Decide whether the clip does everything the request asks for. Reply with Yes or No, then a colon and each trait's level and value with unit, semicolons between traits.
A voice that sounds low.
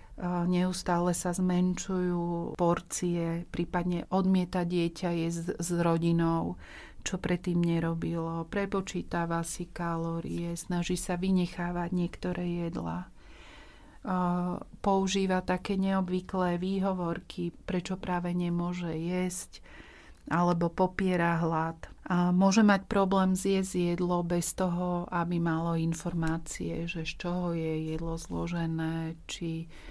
No: medium, 175 Hz